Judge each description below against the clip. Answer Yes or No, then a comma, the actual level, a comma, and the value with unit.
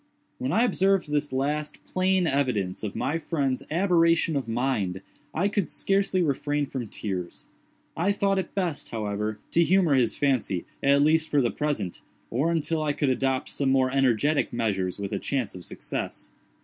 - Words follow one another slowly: No, average, 170 wpm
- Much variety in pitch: Yes, wide, 5.8 semitones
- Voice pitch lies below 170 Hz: Yes, medium, 140 Hz